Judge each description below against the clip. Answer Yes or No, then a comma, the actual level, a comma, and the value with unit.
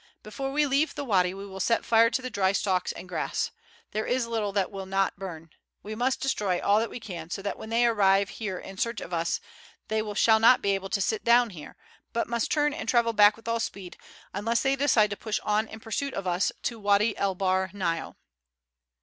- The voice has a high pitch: Yes, high, 210 Hz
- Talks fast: Yes, fast, 225 wpm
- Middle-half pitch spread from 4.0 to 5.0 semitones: No, average, 3.2 semitones